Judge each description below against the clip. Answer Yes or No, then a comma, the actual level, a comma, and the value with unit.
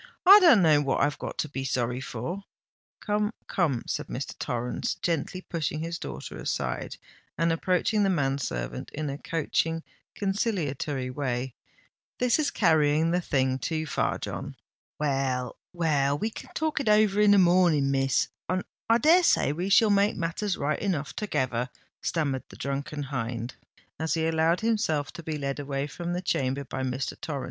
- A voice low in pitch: No, medium, 155 Hz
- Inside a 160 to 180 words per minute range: Yes, average, 165 wpm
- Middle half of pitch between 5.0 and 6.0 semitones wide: Yes, average, 5.3 semitones